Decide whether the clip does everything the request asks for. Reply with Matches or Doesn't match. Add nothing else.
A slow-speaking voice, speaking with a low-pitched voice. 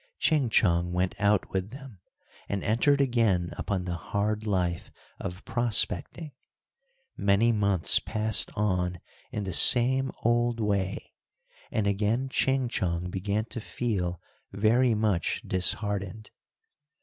Matches